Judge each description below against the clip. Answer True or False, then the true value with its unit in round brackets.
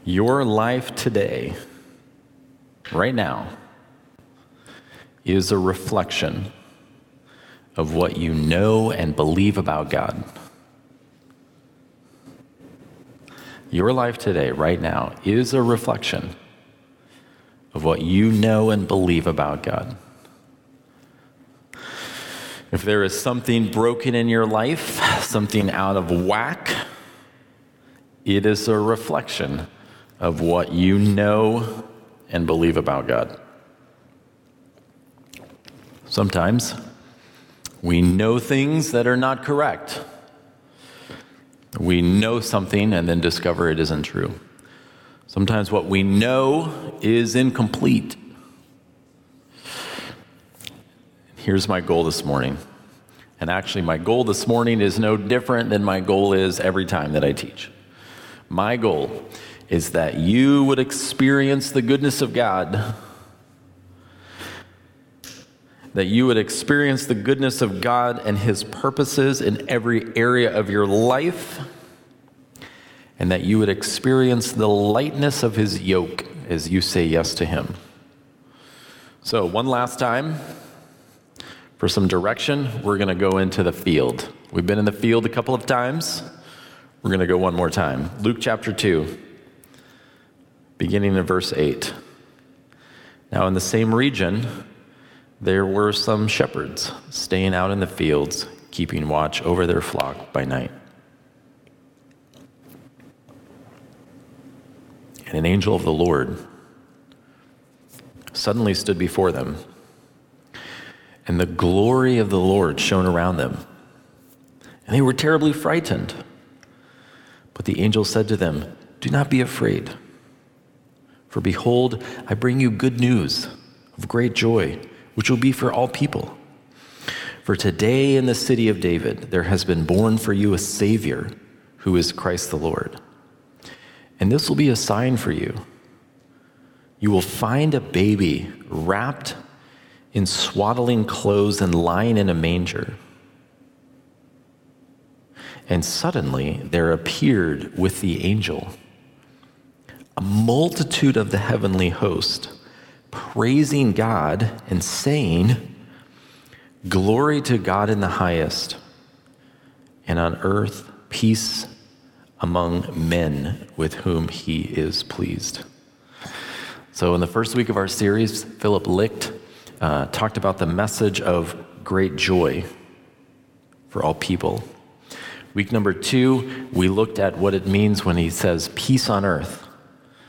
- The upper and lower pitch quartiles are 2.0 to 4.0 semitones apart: False (5.6 semitones)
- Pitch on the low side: True (105 Hz)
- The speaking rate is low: True (120 wpm)